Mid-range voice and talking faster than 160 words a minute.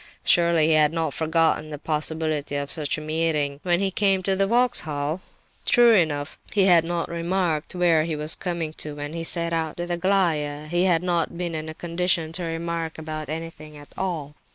Yes: medium, 165 Hz; average, 190 wpm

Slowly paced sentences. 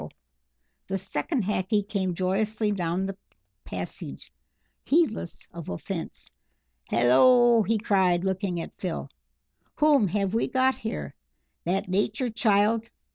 Yes: slow, 115 wpm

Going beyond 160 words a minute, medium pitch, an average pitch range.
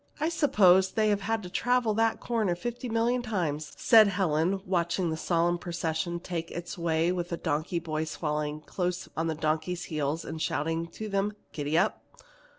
Yes: average, 170 wpm; medium, 175 Hz; average, 4.4 semitones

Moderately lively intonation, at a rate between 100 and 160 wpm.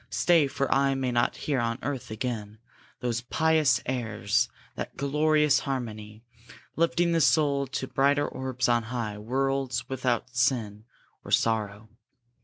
Yes: average, 3.2 semitones; slow, 135 wpm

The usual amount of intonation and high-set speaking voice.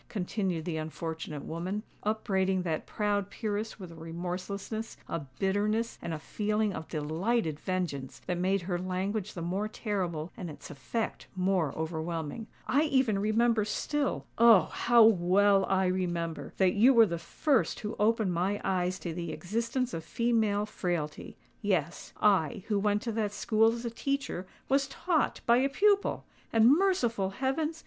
Yes: average, 4.5 semitones; high, 200 Hz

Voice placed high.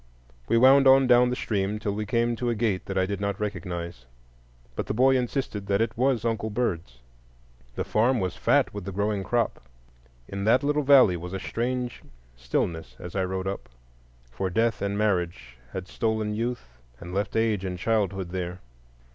No: low, 105 Hz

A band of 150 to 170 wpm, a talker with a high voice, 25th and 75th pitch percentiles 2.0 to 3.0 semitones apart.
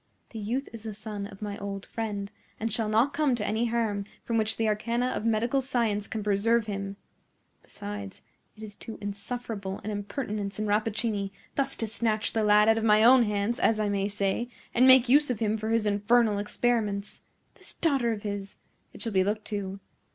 No: average, 200 wpm; high, 215 Hz; narrow, 2.4 semitones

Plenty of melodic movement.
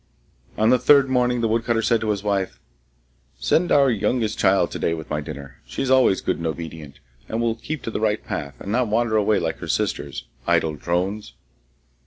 Yes: wide, 6.1 semitones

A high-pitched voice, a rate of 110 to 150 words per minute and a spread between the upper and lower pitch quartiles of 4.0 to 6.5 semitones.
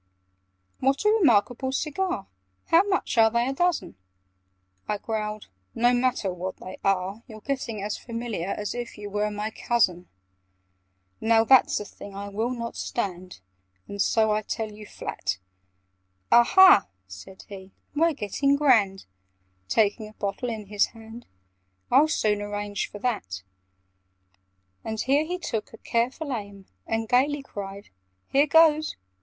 Yes: high, 220 Hz; average, 145 wpm; average, 4.3 semitones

